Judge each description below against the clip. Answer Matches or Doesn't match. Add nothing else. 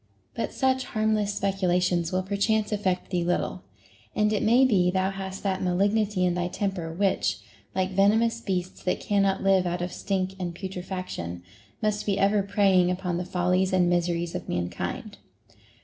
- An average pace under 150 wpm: Doesn't match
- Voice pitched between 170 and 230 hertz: Matches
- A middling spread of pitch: Doesn't match